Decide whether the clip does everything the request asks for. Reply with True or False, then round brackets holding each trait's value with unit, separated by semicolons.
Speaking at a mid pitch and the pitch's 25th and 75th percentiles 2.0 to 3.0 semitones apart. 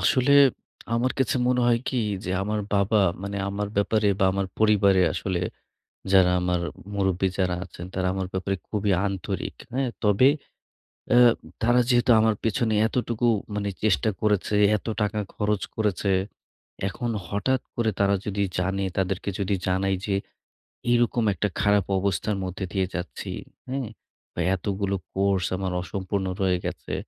False (100 Hz; 2.4 semitones)